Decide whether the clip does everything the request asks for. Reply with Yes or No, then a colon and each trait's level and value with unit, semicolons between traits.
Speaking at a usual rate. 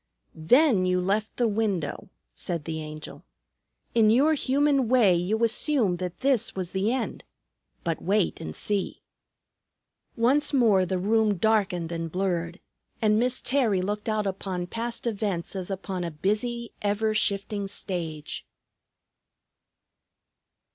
No: slow, 130 wpm